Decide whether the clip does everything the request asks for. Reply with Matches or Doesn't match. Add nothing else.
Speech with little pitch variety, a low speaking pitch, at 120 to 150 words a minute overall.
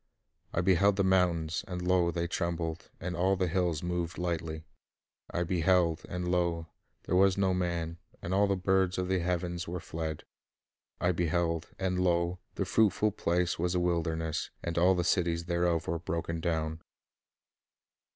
Doesn't match